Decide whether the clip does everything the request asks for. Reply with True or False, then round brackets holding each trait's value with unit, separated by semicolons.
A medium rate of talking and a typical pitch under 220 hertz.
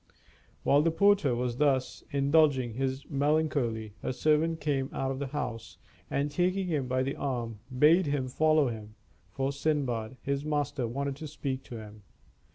True (165 wpm; 140 Hz)